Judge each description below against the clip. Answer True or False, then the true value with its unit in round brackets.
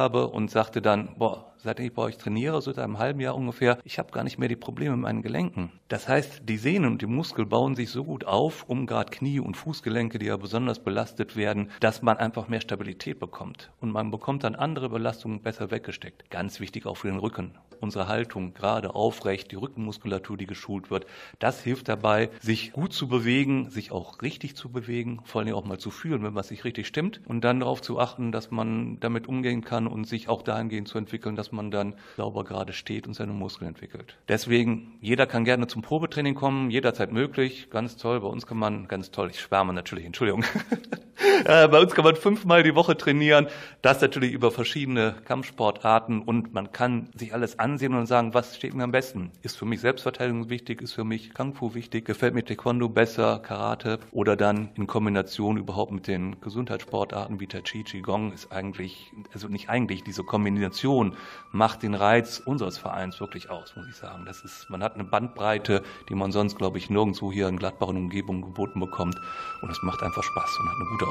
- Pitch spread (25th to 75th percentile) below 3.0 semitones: False (3.4 semitones)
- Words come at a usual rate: False (210 wpm)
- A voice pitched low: True (115 Hz)